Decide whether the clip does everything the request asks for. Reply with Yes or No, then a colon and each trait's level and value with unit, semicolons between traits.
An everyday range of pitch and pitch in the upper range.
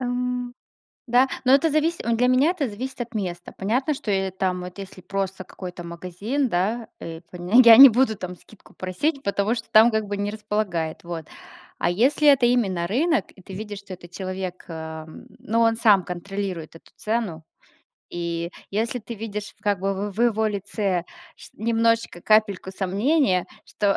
Yes: average, 4.4 semitones; high, 205 Hz